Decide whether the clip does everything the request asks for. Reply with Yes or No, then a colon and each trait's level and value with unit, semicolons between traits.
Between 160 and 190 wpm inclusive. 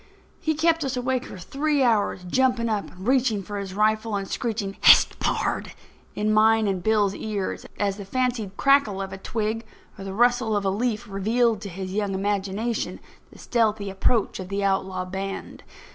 Yes: average, 180 wpm